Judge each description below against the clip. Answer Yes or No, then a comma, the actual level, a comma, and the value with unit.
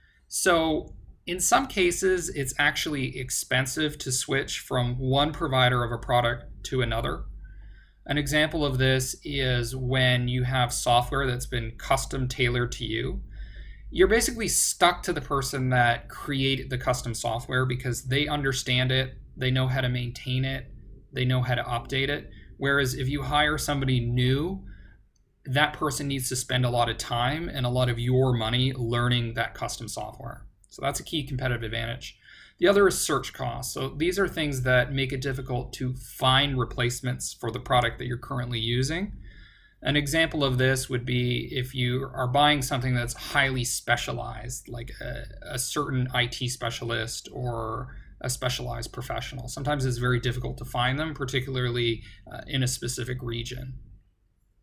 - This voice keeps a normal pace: Yes, average, 165 wpm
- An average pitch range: No, narrow, 2.1 semitones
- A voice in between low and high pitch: No, low, 125 Hz